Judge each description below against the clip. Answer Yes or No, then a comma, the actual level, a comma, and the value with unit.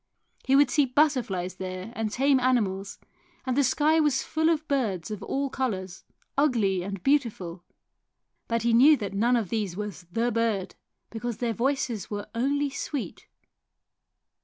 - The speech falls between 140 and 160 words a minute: Yes, average, 155 wpm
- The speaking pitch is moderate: No, high, 235 Hz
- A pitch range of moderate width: No, wide, 5.7 semitones